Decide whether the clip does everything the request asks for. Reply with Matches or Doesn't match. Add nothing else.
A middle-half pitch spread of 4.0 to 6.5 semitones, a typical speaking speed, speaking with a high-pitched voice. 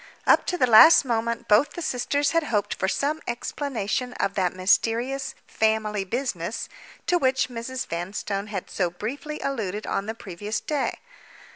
Matches